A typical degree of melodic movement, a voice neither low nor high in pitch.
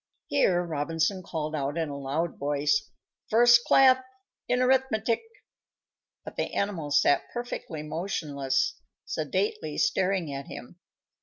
No: wide, 8.2 semitones; medium, 170 Hz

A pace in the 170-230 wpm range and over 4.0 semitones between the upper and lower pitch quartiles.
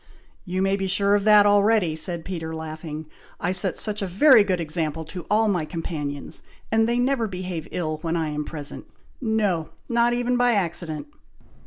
Yes: average, 180 wpm; average, 4.7 semitones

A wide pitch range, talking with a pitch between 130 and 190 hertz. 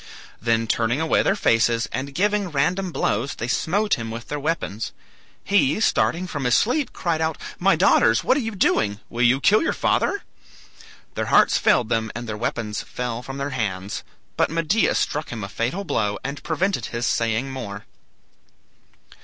Yes: wide, 7.0 semitones; low, 135 Hz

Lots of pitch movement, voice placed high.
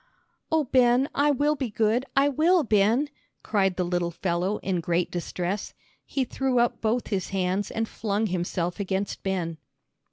Yes: wide, 5.9 semitones; high, 205 Hz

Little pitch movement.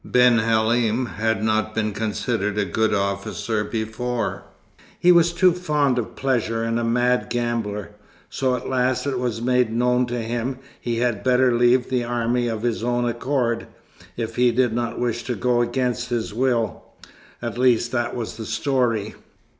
Yes: narrow, 1.9 semitones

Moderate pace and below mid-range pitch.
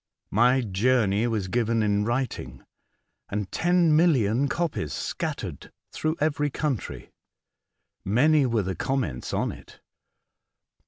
No: slow, 115 wpm; low, 120 Hz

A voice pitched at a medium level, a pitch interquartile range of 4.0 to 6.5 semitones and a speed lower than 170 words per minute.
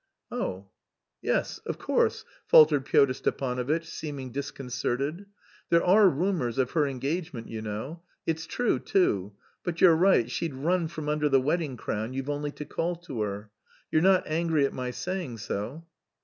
Yes: medium, 145 Hz; average, 5.0 semitones; average, 160 wpm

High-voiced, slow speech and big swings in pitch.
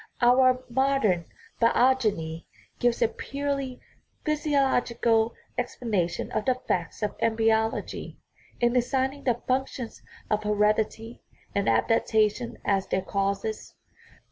No: high, 230 Hz; slow, 105 wpm; average, 3.4 semitones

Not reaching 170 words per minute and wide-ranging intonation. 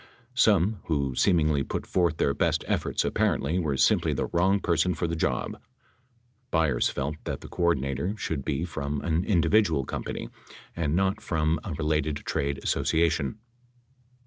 No: average, 155 wpm; average, 3.4 semitones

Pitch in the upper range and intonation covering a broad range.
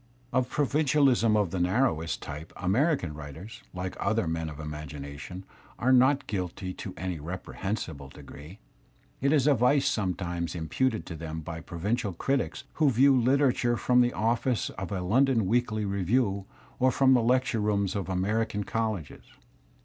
No: low, 105 Hz; wide, 6.4 semitones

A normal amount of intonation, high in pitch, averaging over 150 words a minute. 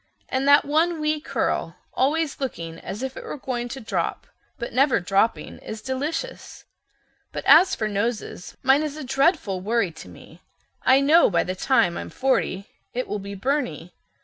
No: wide, 6.2 semitones; very high, 260 Hz; average, 175 wpm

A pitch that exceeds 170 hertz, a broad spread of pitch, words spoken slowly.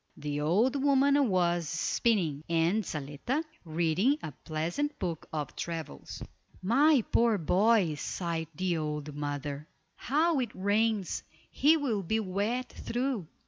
Yes: medium, 185 Hz; wide, 7.3 semitones; slow, 125 wpm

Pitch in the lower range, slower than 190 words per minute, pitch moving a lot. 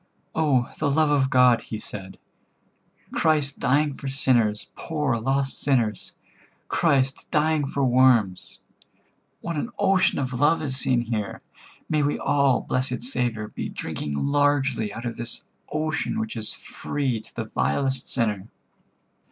No: low, 130 Hz; average, 140 wpm; average, 3.7 semitones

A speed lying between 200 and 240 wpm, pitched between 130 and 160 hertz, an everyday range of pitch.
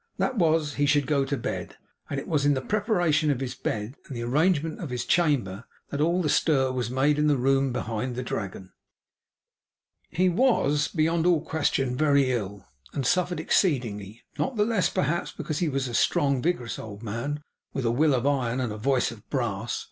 Yes: fast, 205 wpm; medium, 140 Hz; average, 4.3 semitones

